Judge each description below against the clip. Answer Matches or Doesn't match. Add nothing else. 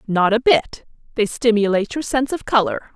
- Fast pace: Doesn't match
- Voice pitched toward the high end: Matches